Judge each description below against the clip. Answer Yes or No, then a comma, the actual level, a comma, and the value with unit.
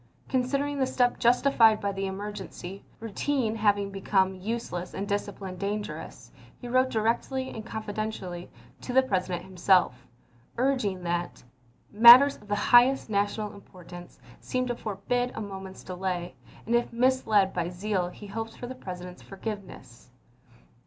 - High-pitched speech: Yes, high, 205 Hz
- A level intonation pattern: No, average, 4.1 semitones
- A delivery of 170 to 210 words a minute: No, average, 145 wpm